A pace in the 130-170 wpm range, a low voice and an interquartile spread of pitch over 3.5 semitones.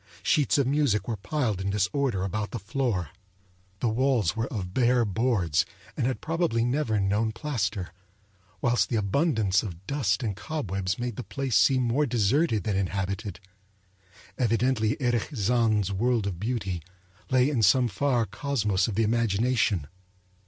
Yes: average, 150 wpm; low, 115 Hz; average, 4.4 semitones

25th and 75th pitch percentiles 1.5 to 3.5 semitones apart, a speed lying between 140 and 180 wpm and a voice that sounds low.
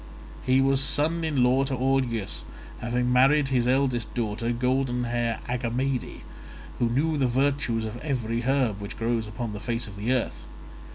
Yes: narrow, 2.5 semitones; average, 165 wpm; low, 125 Hz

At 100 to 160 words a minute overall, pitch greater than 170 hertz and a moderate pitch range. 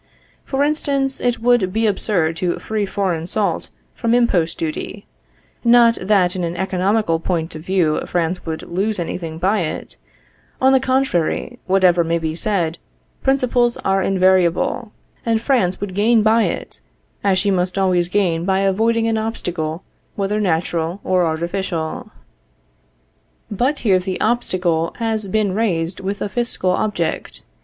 Yes: average, 150 wpm; high, 190 Hz; average, 4.3 semitones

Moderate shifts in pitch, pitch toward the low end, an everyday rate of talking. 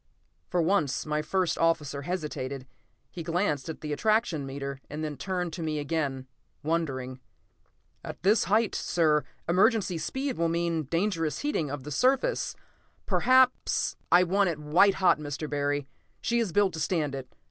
No: average, 4.4 semitones; medium, 165 Hz; average, 160 wpm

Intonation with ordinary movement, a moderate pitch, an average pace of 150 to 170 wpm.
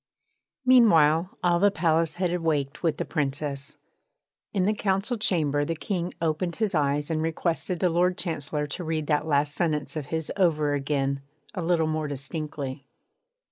Yes: average, 3.2 semitones; medium, 160 Hz; average, 160 wpm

